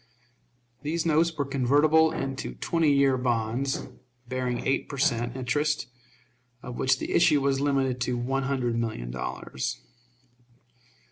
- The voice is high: No, low, 135 Hz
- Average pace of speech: No, slow, 130 wpm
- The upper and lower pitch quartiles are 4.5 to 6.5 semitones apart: No, average, 3.0 semitones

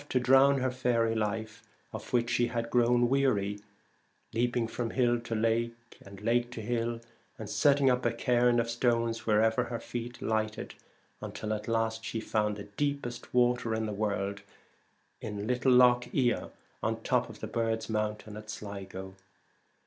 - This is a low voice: Yes, low, 115 Hz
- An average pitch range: No, narrow, 2.1 semitones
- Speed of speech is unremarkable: Yes, average, 165 wpm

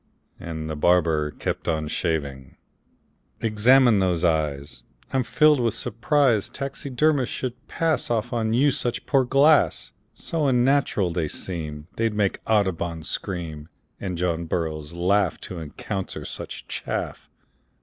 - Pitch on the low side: Yes, very low, 95 Hz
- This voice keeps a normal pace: No, slow, 130 wpm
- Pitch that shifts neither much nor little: No, wide, 7.4 semitones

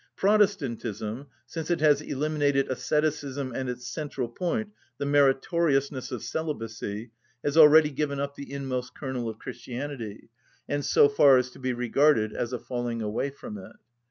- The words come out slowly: No, average, 155 wpm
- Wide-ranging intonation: No, average, 3.3 semitones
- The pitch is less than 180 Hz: Yes, low, 135 Hz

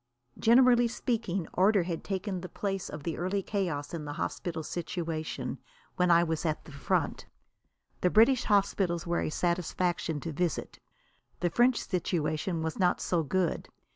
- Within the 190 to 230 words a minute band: No, average, 155 wpm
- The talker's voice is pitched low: No, medium, 175 Hz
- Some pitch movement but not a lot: Yes, average, 3.4 semitones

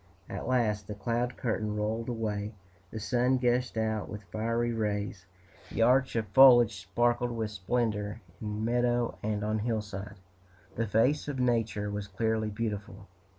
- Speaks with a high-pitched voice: No, low, 110 Hz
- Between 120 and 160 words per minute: Yes, average, 150 wpm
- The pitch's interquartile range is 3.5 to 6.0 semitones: No, narrow, 2.4 semitones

